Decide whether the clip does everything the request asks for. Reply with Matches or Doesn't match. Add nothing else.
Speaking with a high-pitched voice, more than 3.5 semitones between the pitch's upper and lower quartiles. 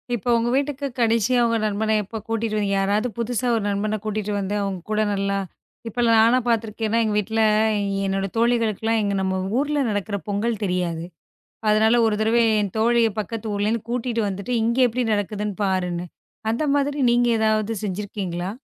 Doesn't match